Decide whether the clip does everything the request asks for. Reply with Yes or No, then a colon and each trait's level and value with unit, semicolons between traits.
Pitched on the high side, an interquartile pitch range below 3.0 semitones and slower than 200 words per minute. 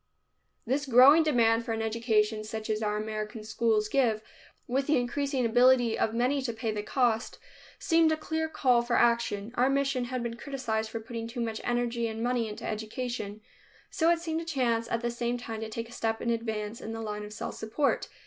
No: high, 235 Hz; narrow, 2.5 semitones; fast, 205 wpm